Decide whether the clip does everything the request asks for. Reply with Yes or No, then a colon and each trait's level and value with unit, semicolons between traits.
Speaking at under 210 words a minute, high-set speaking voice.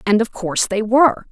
No: fast, 230 wpm; high, 220 Hz